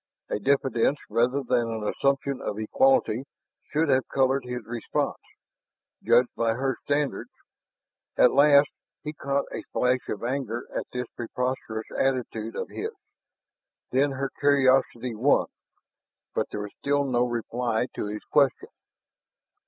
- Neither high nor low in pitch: No, low, 130 Hz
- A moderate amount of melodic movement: Yes, average, 3.0 semitones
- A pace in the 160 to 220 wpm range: No, slow, 135 wpm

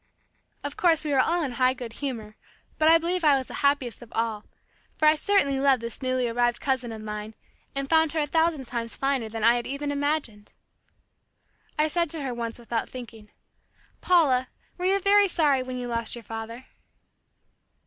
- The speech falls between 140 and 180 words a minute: No, average, 190 wpm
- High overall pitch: Yes, very high, 260 Hz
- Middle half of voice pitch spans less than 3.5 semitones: No, average, 4.7 semitones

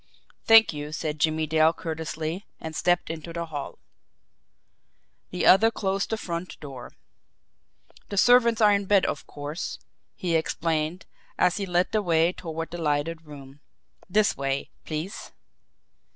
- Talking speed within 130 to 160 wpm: Yes, average, 140 wpm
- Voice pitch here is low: No, medium, 165 Hz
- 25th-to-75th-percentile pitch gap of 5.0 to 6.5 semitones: No, average, 3.5 semitones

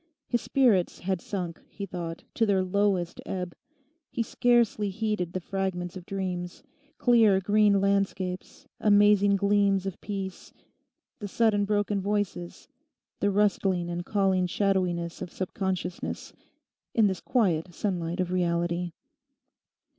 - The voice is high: Yes, high, 195 Hz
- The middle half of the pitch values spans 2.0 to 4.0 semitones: Yes, narrow, 2.4 semitones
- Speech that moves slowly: Yes, slow, 115 wpm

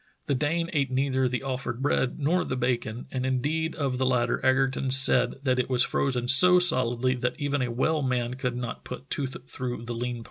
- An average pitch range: No, narrow, 2.0 semitones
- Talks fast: Yes, fast, 210 wpm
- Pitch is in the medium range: No, low, 130 Hz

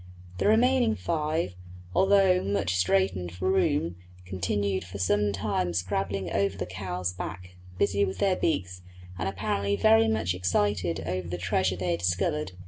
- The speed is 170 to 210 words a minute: No, average, 150 wpm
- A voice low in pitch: Yes, very low, 95 Hz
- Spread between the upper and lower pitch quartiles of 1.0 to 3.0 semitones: Yes, average, 2.7 semitones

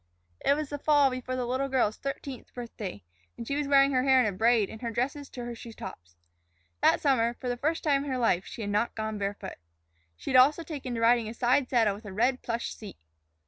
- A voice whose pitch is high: Yes, high, 245 Hz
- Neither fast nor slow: No, fast, 240 wpm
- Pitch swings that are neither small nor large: Yes, average, 3.5 semitones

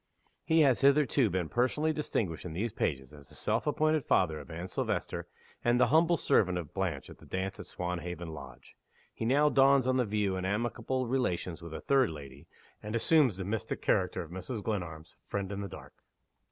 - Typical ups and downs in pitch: No, wide, 6.9 semitones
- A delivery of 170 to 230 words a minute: Yes, average, 195 wpm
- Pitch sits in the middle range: No, low, 100 Hz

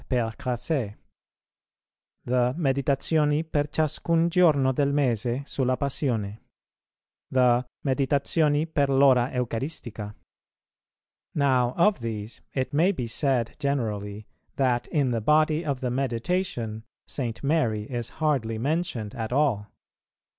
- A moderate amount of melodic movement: Yes, average, 4.0 semitones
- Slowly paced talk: Yes, slow, 110 wpm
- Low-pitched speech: Yes, low, 130 Hz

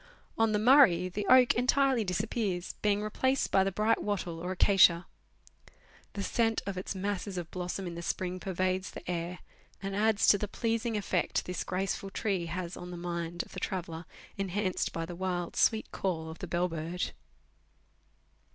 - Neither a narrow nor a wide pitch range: Yes, average, 3.0 semitones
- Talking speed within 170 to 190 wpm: Yes, average, 175 wpm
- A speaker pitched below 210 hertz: Yes, medium, 185 Hz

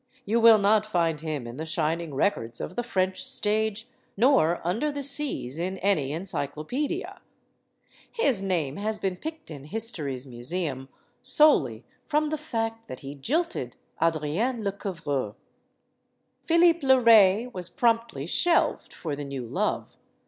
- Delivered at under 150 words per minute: Yes, average, 140 wpm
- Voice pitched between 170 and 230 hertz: Yes, high, 190 Hz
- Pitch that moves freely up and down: Yes, wide, 7.7 semitones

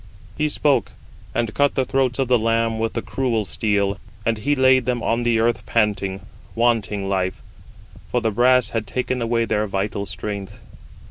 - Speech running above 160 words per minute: Yes, average, 175 wpm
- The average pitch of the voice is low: Yes, low, 115 Hz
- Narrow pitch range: No, average, 3.2 semitones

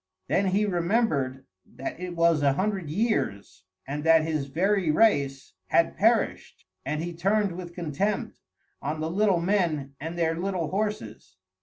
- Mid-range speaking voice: Yes, medium, 170 Hz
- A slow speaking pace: No, average, 150 wpm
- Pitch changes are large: No, average, 4.6 semitones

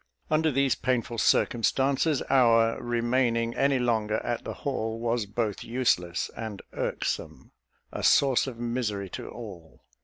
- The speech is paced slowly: Yes, slow, 130 wpm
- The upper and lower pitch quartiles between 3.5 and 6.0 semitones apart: No, narrow, 2.4 semitones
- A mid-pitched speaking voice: No, low, 120 Hz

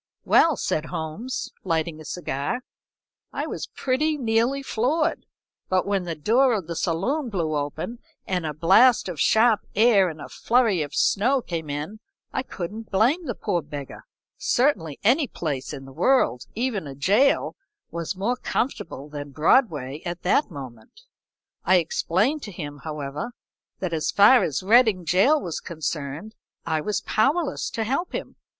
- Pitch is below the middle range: No, medium, 185 Hz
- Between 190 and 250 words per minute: No, average, 155 wpm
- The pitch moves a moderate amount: No, wide, 7.6 semitones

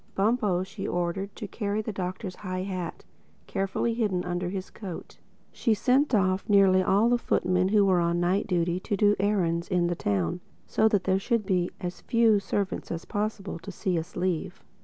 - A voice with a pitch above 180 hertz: Yes, high, 190 Hz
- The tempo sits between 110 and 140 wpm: No, average, 180 wpm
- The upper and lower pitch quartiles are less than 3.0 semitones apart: Yes, narrow, 2.5 semitones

